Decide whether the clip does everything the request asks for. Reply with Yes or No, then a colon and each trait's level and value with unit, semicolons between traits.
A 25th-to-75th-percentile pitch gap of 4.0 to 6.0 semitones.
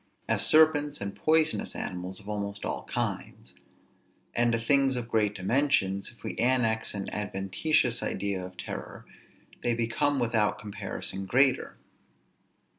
Yes: average, 4.9 semitones